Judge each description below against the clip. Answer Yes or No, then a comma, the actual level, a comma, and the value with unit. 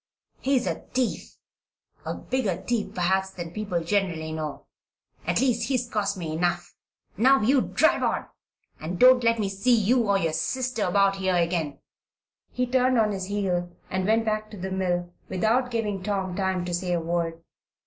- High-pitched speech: Yes, high, 195 Hz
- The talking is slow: No, average, 175 wpm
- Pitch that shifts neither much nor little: Yes, average, 4.6 semitones